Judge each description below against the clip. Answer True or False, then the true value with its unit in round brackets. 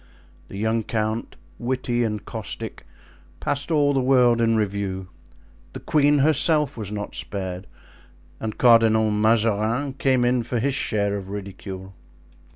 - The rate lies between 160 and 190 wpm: False (135 wpm)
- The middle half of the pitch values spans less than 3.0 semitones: False (3.9 semitones)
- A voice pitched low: True (115 Hz)